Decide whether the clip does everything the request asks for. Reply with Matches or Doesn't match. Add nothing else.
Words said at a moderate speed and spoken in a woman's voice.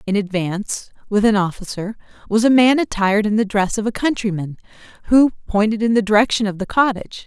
Matches